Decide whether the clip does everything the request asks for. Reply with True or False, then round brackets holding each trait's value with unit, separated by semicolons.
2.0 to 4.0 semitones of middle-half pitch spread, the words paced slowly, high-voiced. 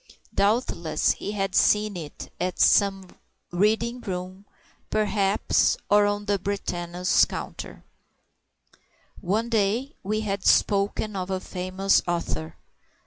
True (2.4 semitones; 105 wpm; 195 Hz)